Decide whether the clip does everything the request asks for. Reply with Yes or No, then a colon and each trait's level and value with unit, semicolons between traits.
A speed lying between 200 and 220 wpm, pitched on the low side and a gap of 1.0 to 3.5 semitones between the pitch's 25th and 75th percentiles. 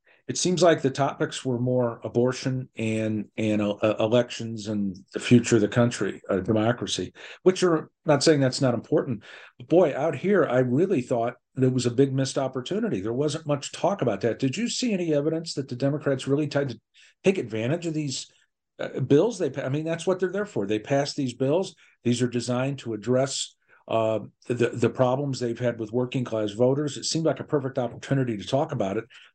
No: fast, 205 wpm; low, 130 Hz; average, 4.1 semitones